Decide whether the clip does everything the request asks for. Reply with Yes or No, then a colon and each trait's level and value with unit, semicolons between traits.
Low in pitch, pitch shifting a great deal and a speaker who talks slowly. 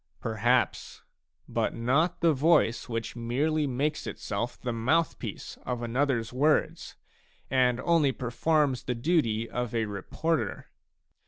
No: low, 125 Hz; average, 4.6 semitones; slow, 120 wpm